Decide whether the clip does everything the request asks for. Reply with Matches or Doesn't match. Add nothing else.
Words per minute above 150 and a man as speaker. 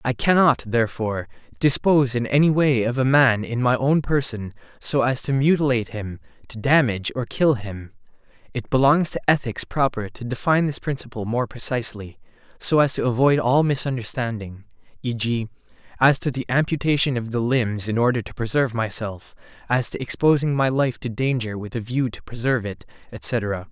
Matches